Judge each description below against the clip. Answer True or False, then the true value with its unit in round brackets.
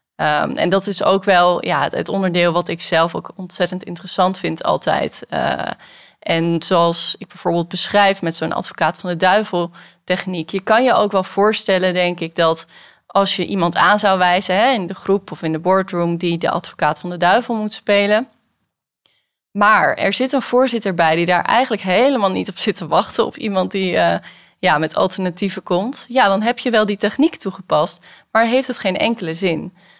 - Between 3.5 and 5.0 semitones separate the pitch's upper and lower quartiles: False (2.9 semitones)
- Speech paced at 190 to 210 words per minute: True (195 wpm)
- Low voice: False (185 Hz)